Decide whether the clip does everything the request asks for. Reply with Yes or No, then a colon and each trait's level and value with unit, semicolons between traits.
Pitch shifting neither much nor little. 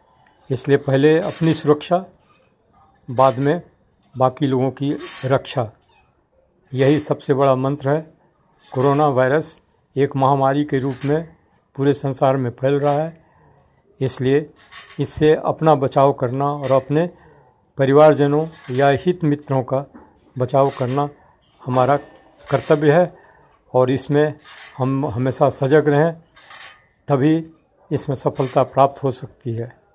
No: narrow, 2.2 semitones